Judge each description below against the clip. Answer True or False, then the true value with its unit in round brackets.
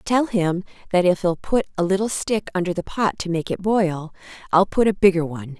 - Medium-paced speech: False (225 wpm)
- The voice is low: False (185 Hz)